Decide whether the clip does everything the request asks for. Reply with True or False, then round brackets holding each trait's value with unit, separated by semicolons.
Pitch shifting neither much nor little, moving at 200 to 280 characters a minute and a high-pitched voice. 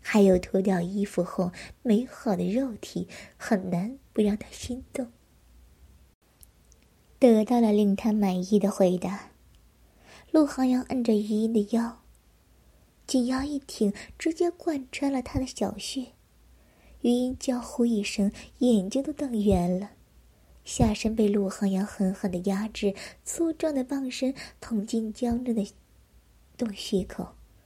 False (4.4 semitones; 190 characters per minute; 215 Hz)